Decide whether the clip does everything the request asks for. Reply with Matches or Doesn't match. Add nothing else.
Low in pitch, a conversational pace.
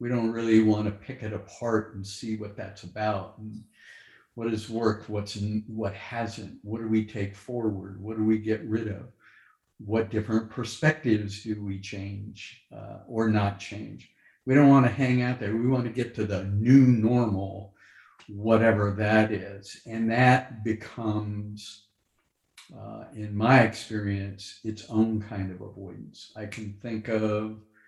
Matches